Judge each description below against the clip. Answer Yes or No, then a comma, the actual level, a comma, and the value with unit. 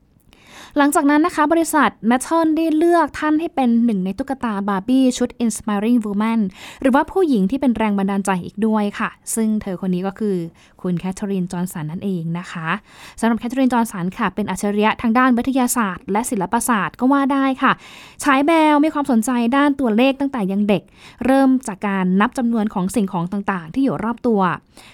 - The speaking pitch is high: Yes, high, 230 Hz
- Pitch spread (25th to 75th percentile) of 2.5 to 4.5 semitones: No, average, 5.2 semitones